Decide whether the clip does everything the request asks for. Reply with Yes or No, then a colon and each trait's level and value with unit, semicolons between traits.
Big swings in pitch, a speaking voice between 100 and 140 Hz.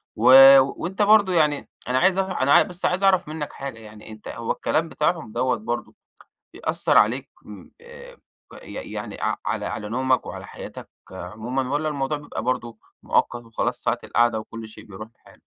Yes: wide, 7.7 semitones; low, 135 Hz